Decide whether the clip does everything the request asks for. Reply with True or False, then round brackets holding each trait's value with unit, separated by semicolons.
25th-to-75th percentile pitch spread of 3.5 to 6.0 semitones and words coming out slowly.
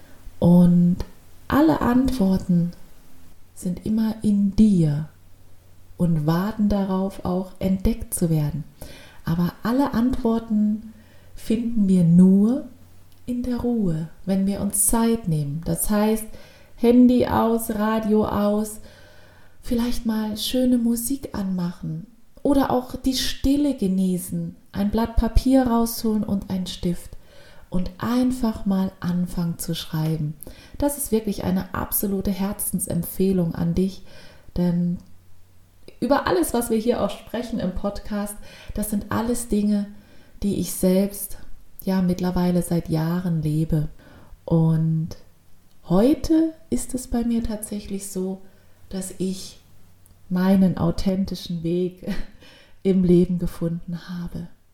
True (4.6 semitones; 115 wpm)